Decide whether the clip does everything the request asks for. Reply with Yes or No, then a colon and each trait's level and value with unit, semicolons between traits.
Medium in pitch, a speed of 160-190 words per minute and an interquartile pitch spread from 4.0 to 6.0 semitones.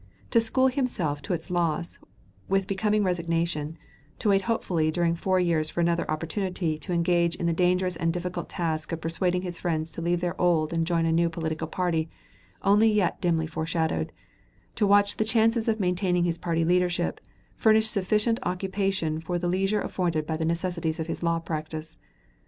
No: medium, 175 Hz; average, 180 wpm; narrow, 2.6 semitones